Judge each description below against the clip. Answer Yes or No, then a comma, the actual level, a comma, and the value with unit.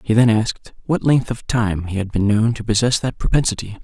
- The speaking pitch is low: Yes, low, 115 Hz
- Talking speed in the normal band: No, fast, 235 wpm